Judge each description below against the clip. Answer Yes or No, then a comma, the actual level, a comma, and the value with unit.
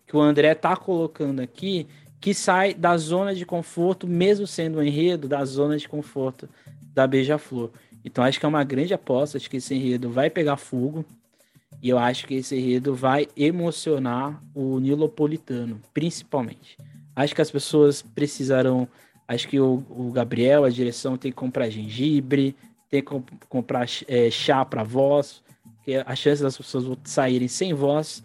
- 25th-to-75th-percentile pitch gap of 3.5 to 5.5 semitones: No, average, 2.9 semitones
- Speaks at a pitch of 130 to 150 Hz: Yes, medium, 140 Hz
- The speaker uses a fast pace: No, average, 170 wpm